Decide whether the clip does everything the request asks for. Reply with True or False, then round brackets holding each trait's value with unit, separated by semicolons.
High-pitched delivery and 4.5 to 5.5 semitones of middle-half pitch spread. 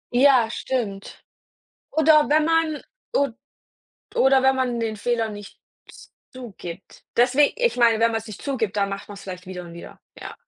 True (235 Hz; 4.9 semitones)